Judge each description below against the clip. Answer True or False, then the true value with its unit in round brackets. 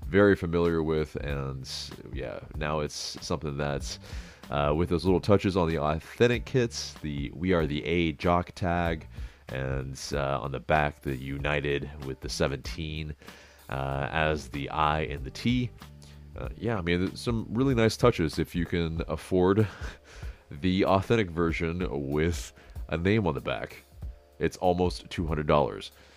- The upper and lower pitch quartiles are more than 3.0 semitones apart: True (3.6 semitones)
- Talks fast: False (150 wpm)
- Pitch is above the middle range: False (80 Hz)